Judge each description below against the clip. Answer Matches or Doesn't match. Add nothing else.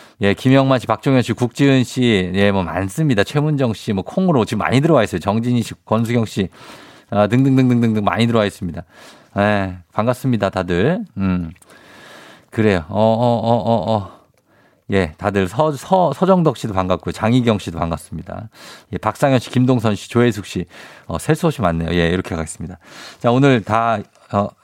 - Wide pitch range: Doesn't match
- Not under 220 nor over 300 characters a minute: Doesn't match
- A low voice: Matches